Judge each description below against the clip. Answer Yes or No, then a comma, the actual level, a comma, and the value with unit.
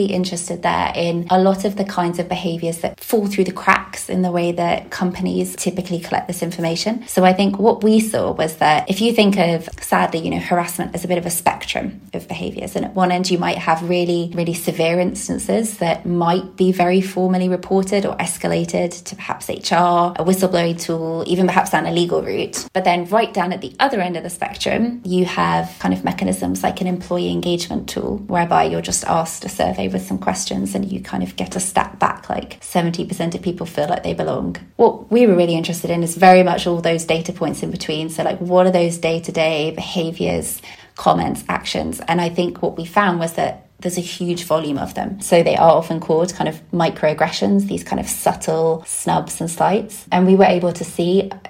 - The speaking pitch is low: No, medium, 175 Hz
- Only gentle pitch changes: Yes, narrow, 2.0 semitones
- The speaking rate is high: Yes, fast, 215 wpm